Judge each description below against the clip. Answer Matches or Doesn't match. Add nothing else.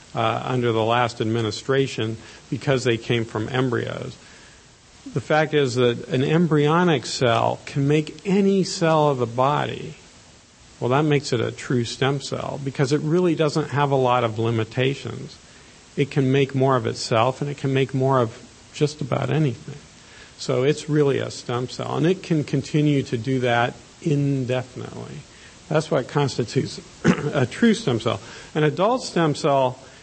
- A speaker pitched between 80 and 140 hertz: Matches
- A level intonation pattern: Doesn't match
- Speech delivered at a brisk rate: Doesn't match